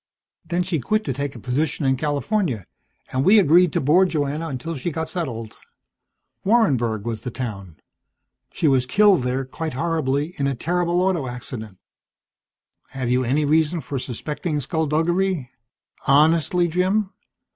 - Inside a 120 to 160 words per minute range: Yes, average, 145 wpm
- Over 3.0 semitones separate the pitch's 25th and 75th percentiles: Yes, average, 5.1 semitones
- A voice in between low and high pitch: Yes, medium, 150 Hz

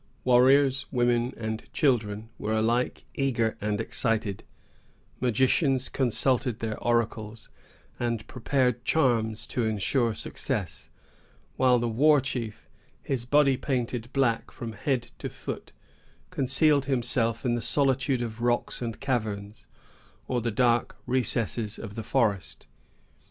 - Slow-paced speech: Yes, slow, 120 wpm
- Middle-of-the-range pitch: No, low, 120 Hz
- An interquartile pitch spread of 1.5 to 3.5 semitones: Yes, average, 2.9 semitones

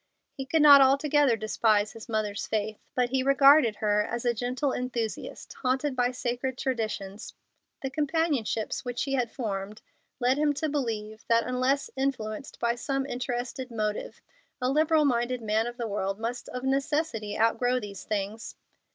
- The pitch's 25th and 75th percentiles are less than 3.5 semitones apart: No, average, 3.8 semitones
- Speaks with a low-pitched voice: No, high, 245 Hz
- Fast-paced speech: No, average, 160 wpm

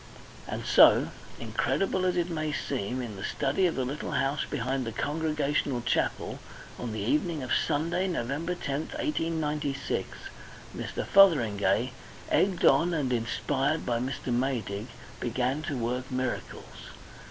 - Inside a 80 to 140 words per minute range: Yes, slow, 135 wpm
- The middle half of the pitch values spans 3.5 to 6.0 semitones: Yes, average, 4.6 semitones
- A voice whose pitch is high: No, medium, 140 Hz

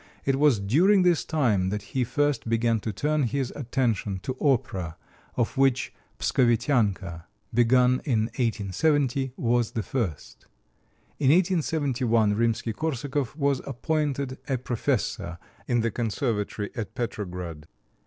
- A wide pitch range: No, average, 4.3 semitones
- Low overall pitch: Yes, low, 120 Hz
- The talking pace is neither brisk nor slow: No, slow, 125 wpm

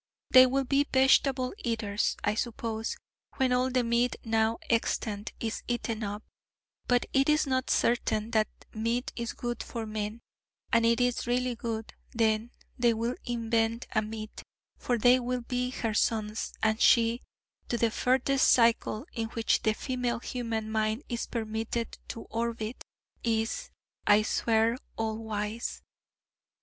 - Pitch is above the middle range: Yes, high, 230 Hz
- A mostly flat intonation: Yes, narrow, 2.0 semitones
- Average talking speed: Yes, average, 150 wpm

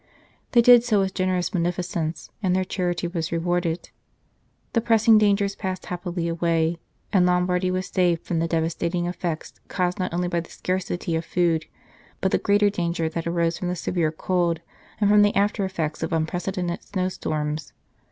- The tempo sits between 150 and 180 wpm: Yes, average, 170 wpm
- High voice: No, medium, 180 Hz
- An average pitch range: No, narrow, 1.9 semitones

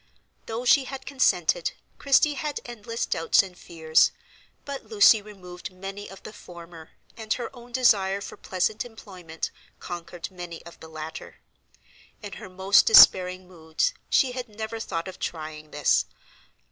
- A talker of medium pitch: No, high, 195 Hz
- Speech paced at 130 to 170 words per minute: Yes, average, 145 wpm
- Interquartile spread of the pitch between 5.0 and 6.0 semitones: Yes, wide, 5.4 semitones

